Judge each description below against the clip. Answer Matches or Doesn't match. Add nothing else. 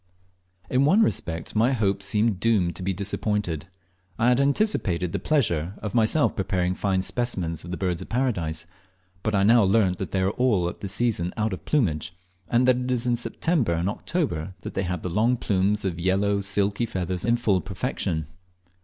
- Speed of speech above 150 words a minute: Matches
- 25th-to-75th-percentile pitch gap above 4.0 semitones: Matches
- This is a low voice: Matches